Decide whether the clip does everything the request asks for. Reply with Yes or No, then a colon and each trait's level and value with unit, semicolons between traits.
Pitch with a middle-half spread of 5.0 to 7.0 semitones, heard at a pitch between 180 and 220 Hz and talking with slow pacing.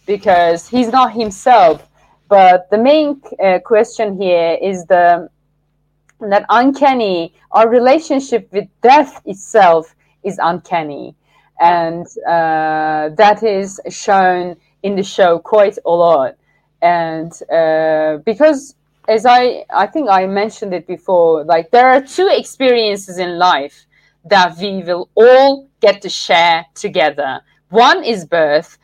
Yes: average, 5.3 semitones; high, 190 Hz; slow, 125 wpm